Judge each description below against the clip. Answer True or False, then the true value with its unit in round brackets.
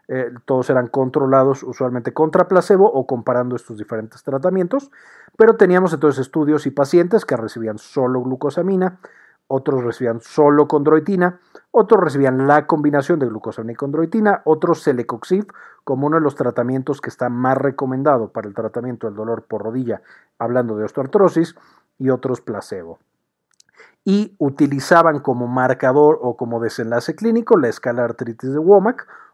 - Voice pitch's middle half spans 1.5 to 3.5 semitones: False (4.9 semitones)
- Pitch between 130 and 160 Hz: True (135 Hz)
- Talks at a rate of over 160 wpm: False (145 wpm)